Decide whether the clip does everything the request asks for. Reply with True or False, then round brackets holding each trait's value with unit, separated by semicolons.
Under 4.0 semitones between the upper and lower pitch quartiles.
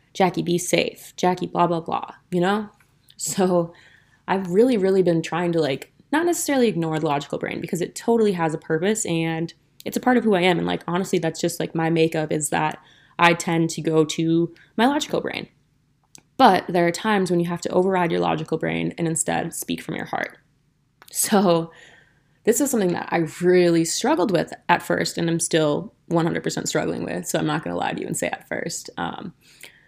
True (2.6 semitones)